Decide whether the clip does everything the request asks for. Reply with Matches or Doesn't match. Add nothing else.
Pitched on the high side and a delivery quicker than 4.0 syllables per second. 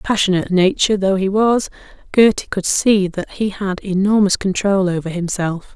Matches